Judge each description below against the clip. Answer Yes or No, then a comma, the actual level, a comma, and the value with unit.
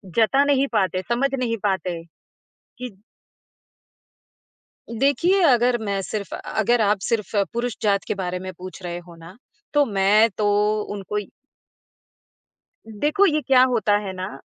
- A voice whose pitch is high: Yes, high, 215 Hz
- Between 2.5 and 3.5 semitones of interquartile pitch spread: No, average, 4.6 semitones